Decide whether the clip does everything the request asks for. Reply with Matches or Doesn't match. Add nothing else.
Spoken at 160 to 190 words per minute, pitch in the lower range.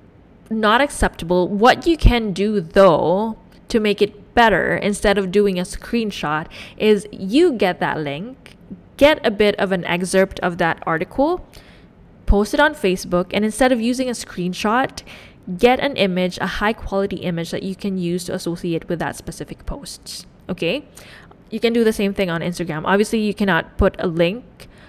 Doesn't match